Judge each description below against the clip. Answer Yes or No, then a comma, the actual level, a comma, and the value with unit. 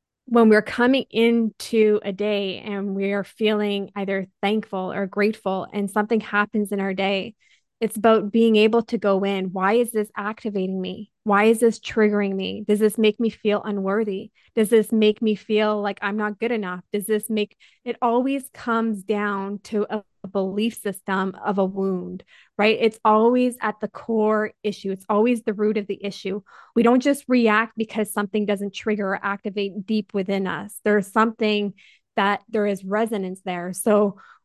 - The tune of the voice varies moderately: No, narrow, 1.8 semitones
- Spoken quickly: No, average, 180 wpm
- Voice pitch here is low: No, high, 210 Hz